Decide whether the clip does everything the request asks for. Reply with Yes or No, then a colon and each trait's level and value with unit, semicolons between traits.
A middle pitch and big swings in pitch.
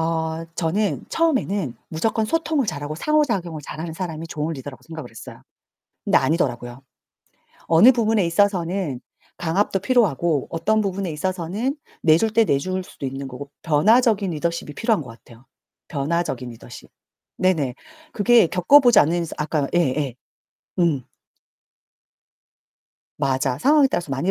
Yes: medium, 170 Hz; wide, 5.8 semitones